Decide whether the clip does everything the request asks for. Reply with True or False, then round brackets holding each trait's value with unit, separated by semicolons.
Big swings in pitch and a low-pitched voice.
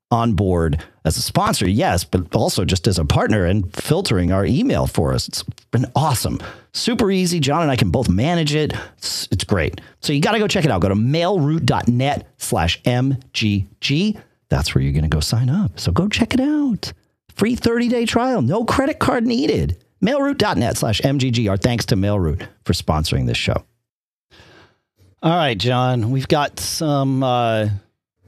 True (8.4 semitones; 125 Hz)